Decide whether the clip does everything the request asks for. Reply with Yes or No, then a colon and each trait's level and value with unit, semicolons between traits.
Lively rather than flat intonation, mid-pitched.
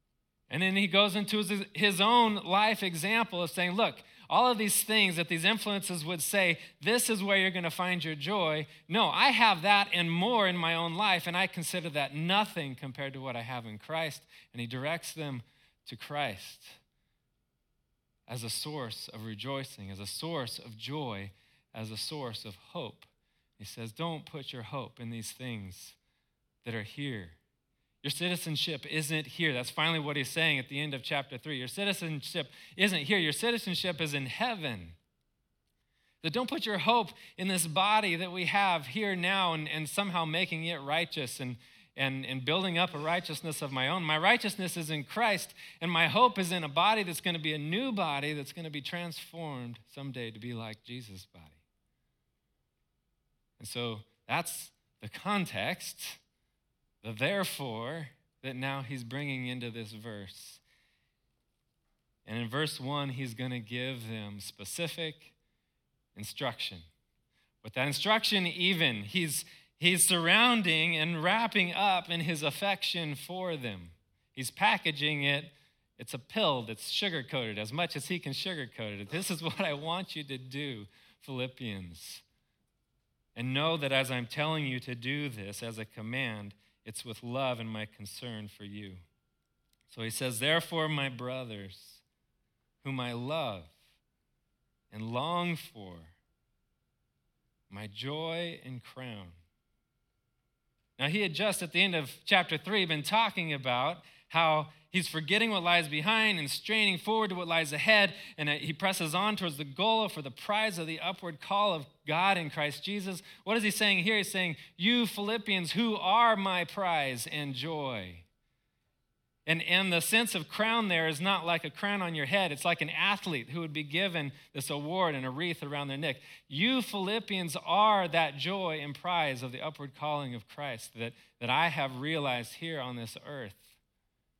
Yes: wide, 6.4 semitones; medium, 155 Hz